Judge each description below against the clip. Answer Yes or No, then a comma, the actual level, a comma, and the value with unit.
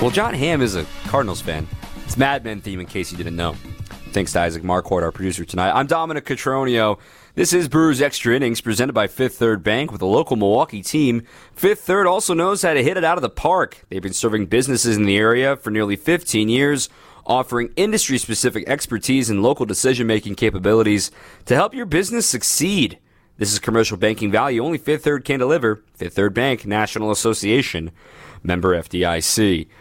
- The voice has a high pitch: No, low, 115 Hz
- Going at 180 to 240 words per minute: Yes, average, 190 wpm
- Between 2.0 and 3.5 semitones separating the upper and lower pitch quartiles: No, average, 5.3 semitones